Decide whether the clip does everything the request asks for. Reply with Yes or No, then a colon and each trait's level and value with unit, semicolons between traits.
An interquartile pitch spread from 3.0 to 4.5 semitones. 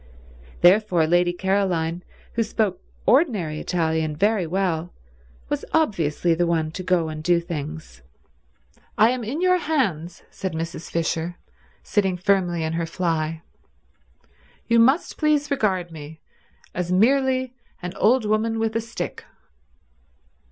No: average, 5.3 semitones